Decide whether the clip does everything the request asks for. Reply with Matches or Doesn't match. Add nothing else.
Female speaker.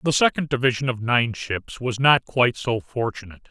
Doesn't match